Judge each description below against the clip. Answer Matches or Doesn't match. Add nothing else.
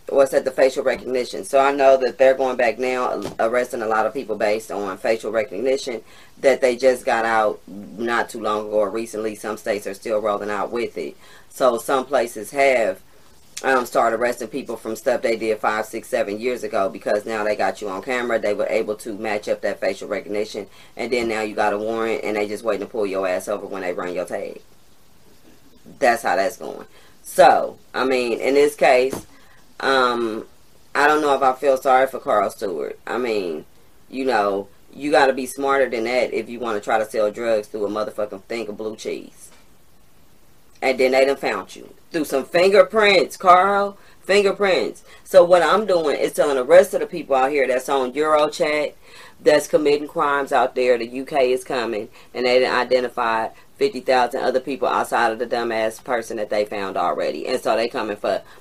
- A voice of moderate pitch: Doesn't match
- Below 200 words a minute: Doesn't match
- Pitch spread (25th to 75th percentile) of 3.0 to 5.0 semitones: Matches